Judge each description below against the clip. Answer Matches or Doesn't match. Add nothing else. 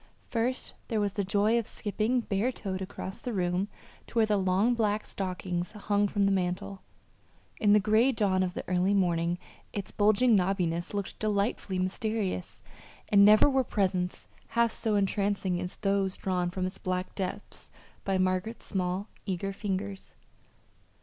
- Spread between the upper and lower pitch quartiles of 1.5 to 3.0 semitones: Matches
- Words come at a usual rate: Matches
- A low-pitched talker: Doesn't match